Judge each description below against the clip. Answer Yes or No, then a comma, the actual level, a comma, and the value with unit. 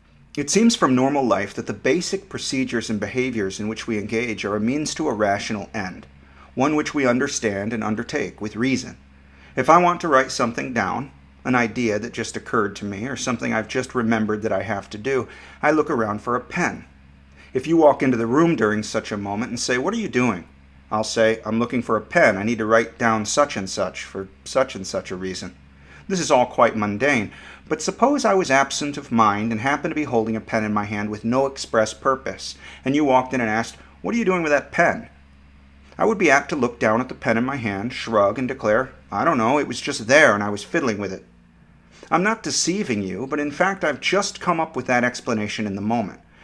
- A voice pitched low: Yes, low, 115 Hz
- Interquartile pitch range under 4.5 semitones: No, average, 4.9 semitones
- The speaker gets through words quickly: Yes, fast, 235 wpm